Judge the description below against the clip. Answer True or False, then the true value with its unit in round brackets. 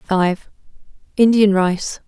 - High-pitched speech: True (200 Hz)